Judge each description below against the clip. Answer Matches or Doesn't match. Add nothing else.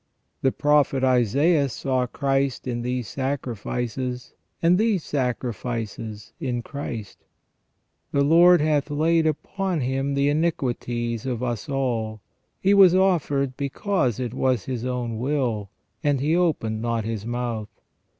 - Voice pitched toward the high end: Doesn't match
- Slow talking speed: Matches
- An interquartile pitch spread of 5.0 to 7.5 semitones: Doesn't match